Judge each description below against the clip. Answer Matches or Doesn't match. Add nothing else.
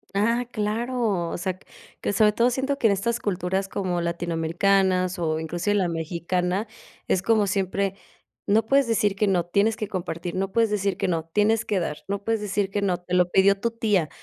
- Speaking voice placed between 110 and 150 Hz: Doesn't match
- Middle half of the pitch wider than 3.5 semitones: Doesn't match